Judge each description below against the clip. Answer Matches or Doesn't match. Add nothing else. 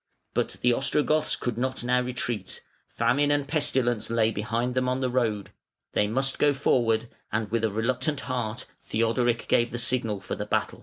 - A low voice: Matches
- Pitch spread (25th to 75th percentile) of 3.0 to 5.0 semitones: Doesn't match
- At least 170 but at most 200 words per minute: Matches